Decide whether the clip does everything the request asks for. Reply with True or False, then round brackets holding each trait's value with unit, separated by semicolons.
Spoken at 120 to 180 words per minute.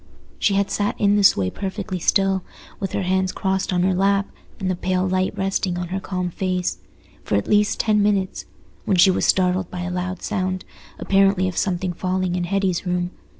False (195 wpm)